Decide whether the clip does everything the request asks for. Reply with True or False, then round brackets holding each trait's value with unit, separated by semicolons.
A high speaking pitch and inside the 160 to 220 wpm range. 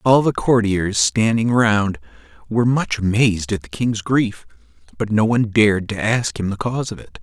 False (110 Hz; 190 wpm)